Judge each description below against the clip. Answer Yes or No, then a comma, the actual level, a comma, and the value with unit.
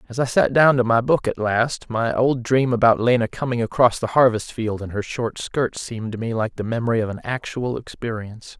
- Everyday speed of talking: No, fast, 230 wpm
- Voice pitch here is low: Yes, low, 120 Hz